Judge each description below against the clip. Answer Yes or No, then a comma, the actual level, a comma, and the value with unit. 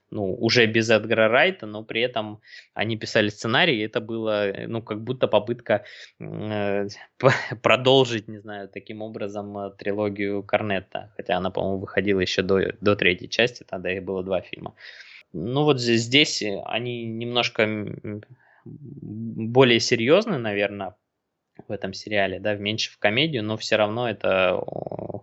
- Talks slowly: No, average, 140 wpm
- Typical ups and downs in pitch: No, narrow, 2.2 semitones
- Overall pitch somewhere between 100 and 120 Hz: Yes, low, 110 Hz